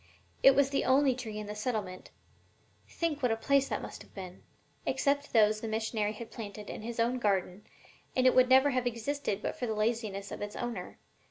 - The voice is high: Yes, high, 230 Hz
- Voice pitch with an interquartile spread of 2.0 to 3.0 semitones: No, average, 3.6 semitones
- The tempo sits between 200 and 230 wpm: Yes, fast, 205 wpm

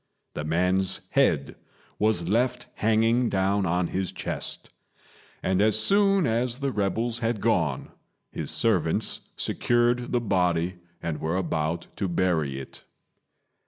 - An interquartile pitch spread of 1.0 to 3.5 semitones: No, average, 5.3 semitones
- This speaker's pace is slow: Yes, slow, 125 wpm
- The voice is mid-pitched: No, low, 100 Hz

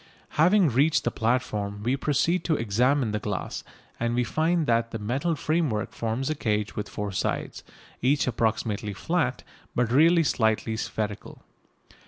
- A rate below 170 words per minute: Yes, average, 150 wpm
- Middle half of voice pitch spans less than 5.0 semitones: No, wide, 5.5 semitones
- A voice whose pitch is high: No, low, 120 Hz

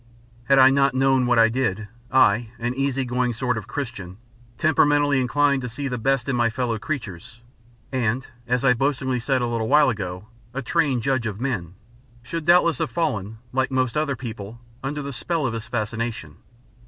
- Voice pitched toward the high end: No, low, 125 Hz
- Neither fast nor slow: Yes, average, 185 wpm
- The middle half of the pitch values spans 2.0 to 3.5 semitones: Yes, average, 3.1 semitones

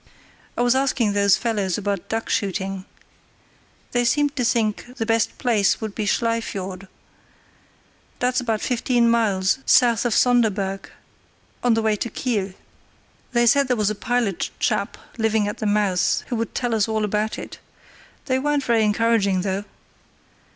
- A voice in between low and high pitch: No, high, 225 Hz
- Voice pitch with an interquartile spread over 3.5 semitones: No, average, 3.0 semitones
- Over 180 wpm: No, average, 160 wpm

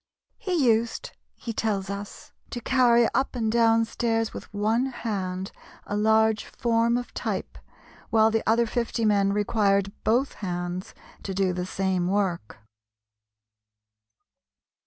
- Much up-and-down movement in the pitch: No, average, 2.9 semitones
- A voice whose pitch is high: Yes, high, 220 Hz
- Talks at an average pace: No, slow, 130 wpm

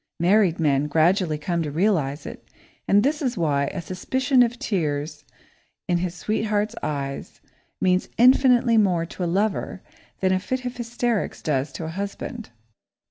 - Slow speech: No, average, 155 wpm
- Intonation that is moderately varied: No, wide, 6.1 semitones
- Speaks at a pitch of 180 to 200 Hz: Yes, medium, 185 Hz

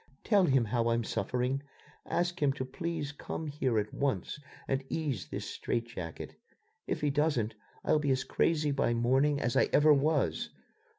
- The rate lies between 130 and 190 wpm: Yes, average, 170 wpm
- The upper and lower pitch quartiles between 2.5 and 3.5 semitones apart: No, average, 4.1 semitones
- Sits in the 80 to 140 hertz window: Yes, low, 135 Hz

